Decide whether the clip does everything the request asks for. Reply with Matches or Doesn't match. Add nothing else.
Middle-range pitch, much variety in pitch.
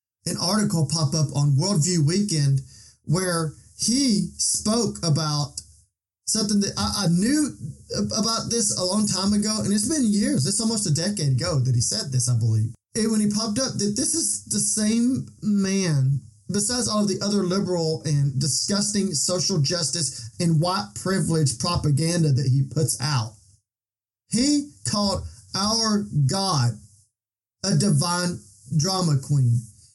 Matches